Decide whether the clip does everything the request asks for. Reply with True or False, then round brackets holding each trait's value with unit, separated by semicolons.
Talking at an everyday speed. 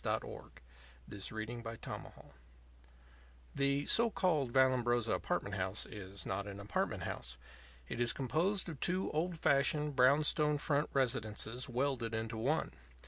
False (130 wpm)